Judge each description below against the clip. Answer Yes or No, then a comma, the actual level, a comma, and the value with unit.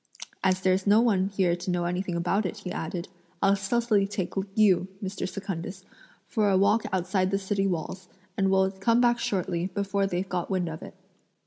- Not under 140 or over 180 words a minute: No, average, 190 wpm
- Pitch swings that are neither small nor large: No, narrow, 1.7 semitones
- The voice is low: No, high, 190 Hz